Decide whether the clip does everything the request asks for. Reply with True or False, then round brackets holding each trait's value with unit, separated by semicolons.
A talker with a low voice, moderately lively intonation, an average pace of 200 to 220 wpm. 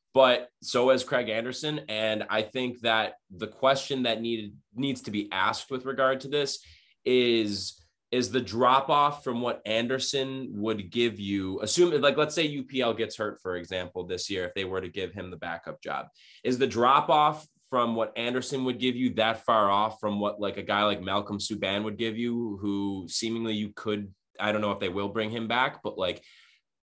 True (115 Hz; 3.9 semitones; 205 wpm)